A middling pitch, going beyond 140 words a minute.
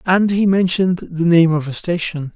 Yes: medium, 175 Hz; fast, 205 wpm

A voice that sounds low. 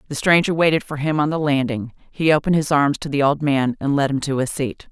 No: medium, 145 Hz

